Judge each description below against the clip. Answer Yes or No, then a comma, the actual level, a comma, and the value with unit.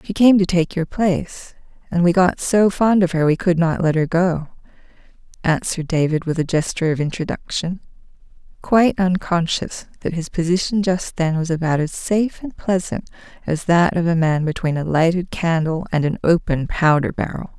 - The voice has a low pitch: No, medium, 170 Hz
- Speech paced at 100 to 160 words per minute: No, average, 180 wpm